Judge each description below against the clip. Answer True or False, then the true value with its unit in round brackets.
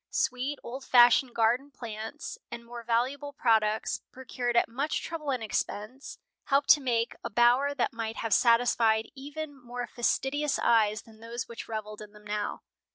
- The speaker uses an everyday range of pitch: True (3.2 semitones)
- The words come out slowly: False (160 wpm)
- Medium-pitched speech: False (240 Hz)